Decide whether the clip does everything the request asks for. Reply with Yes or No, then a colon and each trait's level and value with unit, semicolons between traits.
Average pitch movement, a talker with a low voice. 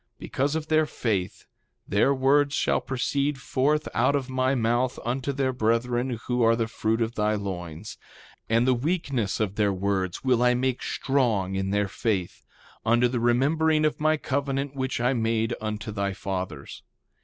Yes: average, 4.2 semitones; low, 120 Hz